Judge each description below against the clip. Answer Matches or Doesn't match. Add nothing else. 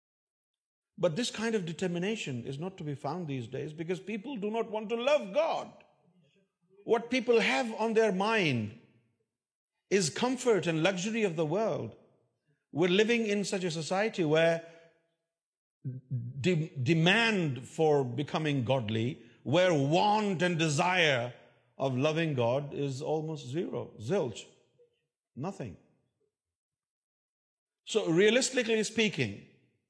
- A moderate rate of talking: Doesn't match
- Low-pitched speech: Doesn't match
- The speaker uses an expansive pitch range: Matches